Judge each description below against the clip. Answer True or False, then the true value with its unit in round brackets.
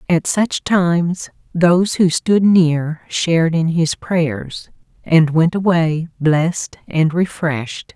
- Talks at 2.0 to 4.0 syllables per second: True (3.4 syllables/s)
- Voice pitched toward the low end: False (165 Hz)